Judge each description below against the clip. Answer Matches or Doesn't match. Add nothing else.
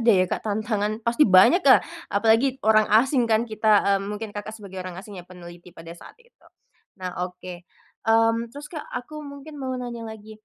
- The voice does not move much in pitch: Doesn't match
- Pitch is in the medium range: Doesn't match